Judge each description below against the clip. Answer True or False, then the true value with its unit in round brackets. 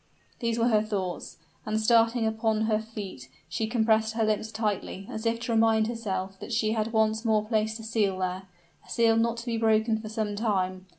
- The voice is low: False (220 Hz)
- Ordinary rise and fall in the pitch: False (1.2 semitones)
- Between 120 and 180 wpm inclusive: False (200 wpm)